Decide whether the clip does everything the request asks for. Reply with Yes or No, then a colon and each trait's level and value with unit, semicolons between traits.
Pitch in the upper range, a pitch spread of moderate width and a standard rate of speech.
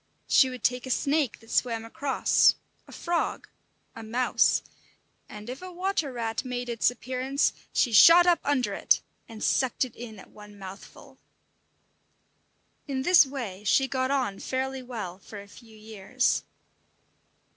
Yes: very high, 250 Hz; average, 3.5 semitones; average, 150 wpm